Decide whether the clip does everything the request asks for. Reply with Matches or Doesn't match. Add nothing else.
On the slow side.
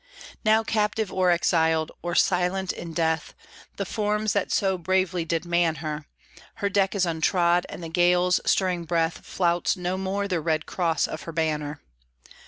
Doesn't match